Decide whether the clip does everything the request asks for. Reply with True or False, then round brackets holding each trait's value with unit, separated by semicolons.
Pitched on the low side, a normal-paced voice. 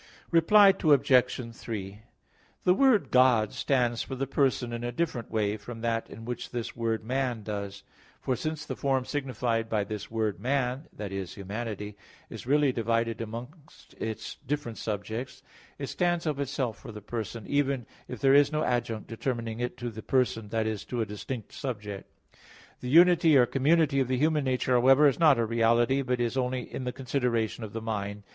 True (120 Hz; 185 wpm)